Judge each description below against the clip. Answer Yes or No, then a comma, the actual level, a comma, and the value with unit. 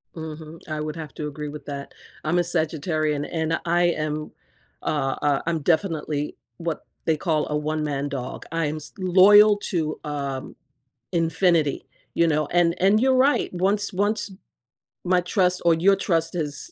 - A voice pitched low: No, medium, 160 Hz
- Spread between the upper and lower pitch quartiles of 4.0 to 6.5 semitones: No, average, 2.9 semitones